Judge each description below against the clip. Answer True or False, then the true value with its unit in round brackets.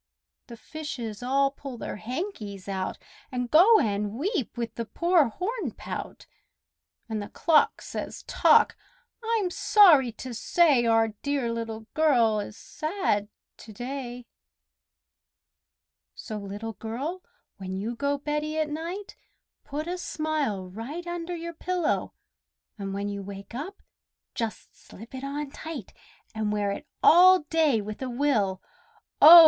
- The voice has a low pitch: False (260 Hz)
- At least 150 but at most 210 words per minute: False (135 wpm)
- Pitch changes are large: True (6.4 semitones)